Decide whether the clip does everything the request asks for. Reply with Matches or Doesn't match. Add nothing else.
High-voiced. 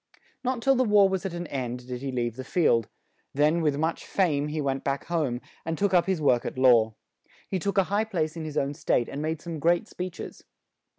Doesn't match